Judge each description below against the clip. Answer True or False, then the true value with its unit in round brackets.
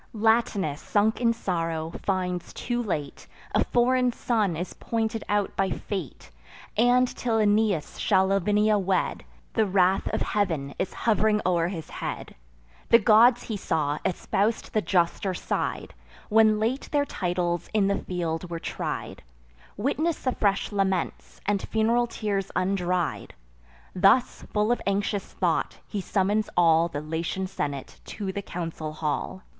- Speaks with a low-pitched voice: False (195 Hz)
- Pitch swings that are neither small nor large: True (3.8 semitones)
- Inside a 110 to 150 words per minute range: True (140 wpm)